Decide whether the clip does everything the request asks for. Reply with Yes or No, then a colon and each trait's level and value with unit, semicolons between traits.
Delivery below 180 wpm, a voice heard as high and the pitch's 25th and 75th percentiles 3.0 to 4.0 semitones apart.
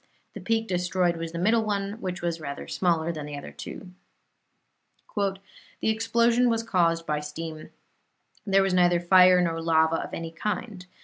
No: average, 165 wpm; medium, 180 Hz; average, 3.6 semitones